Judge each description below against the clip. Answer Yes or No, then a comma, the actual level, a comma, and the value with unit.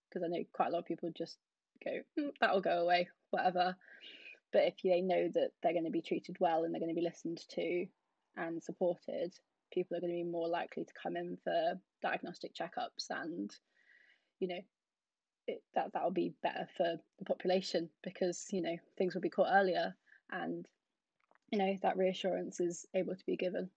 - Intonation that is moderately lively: No, narrow, 1.8 semitones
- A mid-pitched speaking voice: Yes, medium, 180 Hz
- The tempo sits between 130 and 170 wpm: No, average, 195 wpm